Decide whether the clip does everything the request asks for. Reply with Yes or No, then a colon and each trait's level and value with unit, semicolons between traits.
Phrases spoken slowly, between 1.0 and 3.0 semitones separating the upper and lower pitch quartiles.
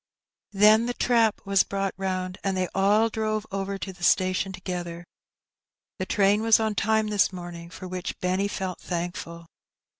No: average, 160 wpm; narrow, 2.4 semitones